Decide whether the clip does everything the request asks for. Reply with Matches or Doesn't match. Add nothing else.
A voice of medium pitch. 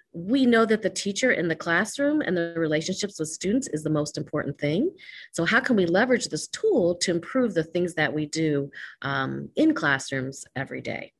Matches